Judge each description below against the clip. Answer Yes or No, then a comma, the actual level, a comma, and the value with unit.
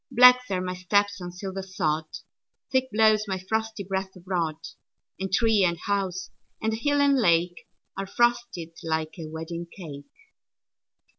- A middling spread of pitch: Yes, average, 4.2 semitones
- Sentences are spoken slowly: Yes, slow, 130 wpm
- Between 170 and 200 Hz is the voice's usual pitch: Yes, high, 190 Hz